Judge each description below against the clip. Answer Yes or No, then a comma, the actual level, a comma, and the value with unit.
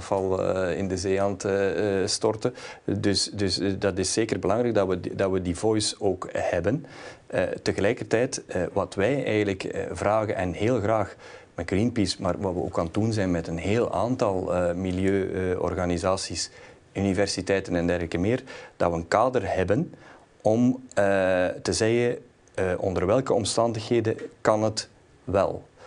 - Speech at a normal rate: Yes, average, 155 wpm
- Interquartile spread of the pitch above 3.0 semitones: No, average, 2.7 semitones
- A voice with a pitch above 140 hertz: No, low, 100 Hz